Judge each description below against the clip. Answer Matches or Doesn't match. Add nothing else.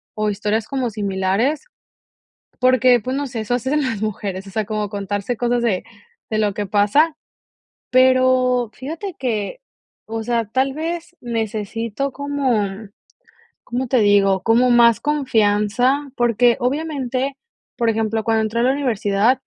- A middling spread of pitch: Matches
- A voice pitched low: Doesn't match